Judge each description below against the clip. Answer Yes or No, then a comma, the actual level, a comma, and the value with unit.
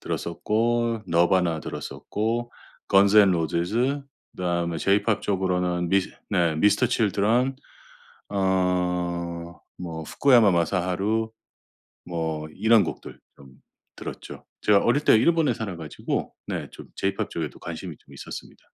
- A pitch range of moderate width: Yes, average, 4.3 semitones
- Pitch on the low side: Yes, very low, 95 Hz